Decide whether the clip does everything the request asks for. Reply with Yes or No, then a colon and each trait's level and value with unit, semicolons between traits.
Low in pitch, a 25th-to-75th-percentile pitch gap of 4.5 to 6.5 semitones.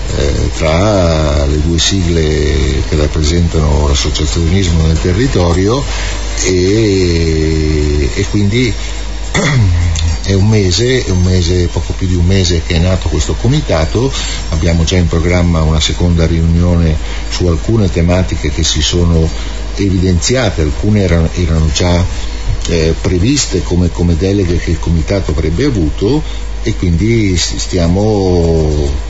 No: very low, 85 Hz; average, 3.3 semitones